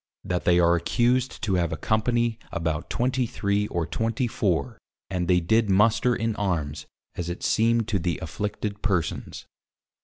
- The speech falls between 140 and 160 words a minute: Yes, average, 150 wpm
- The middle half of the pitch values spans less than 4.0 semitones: No, average, 4.7 semitones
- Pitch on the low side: Yes, low, 100 Hz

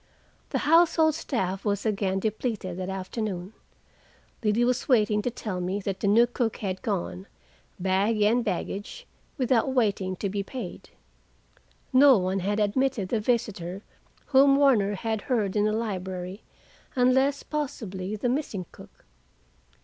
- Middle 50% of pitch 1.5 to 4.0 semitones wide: No, average, 4.5 semitones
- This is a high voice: Yes, high, 210 Hz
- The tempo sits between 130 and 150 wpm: Yes, average, 140 wpm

